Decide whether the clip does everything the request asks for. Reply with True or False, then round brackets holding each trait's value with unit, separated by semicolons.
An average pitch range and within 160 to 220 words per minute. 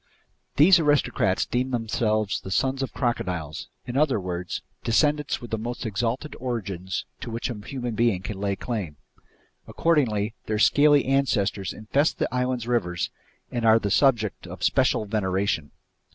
False (4.6 semitones; 150 wpm)